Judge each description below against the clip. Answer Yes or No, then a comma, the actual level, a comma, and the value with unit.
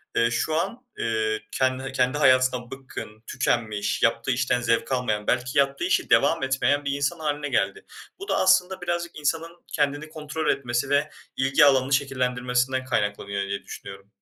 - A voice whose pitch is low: Yes, low, 130 Hz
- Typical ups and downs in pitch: Yes, average, 3.4 semitones